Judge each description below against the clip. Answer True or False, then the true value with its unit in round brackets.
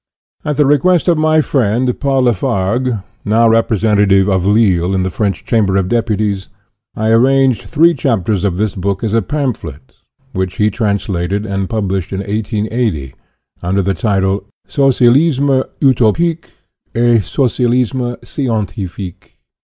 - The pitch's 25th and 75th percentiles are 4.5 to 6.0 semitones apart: True (4.8 semitones)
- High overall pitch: False (110 Hz)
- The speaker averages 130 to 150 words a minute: True (140 wpm)